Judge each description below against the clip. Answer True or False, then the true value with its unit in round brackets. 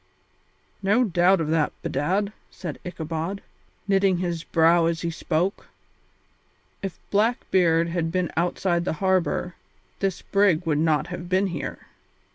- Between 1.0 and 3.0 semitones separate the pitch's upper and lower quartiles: True (2.7 semitones)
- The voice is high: False (175 Hz)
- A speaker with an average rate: False (130 wpm)